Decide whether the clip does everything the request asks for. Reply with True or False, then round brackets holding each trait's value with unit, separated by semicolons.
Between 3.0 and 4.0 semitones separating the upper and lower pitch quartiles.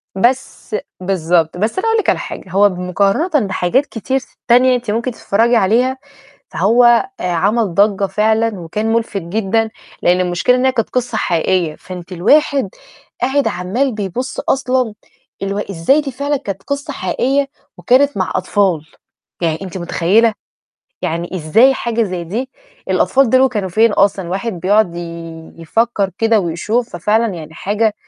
False (5.3 semitones)